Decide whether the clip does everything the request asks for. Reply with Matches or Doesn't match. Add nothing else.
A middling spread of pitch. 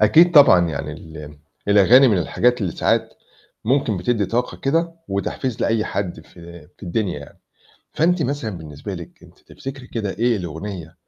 Doesn't match